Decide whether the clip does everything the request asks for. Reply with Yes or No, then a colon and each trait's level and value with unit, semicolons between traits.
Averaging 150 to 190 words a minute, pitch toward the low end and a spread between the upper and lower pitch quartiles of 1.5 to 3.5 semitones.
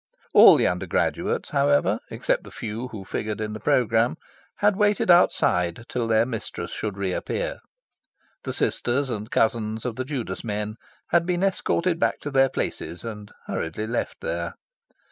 No: average, 160 wpm; low, 115 Hz; average, 5.1 semitones